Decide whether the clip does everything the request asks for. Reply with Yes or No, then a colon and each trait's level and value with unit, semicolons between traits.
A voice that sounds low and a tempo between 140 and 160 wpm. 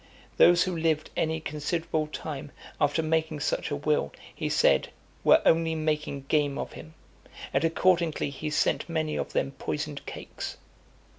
No: medium, 155 Hz; average, 150 wpm